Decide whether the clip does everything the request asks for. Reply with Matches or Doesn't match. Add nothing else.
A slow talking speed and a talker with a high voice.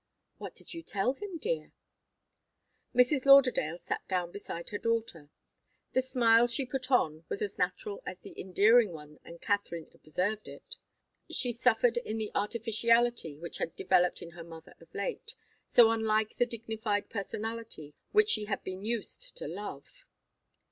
Doesn't match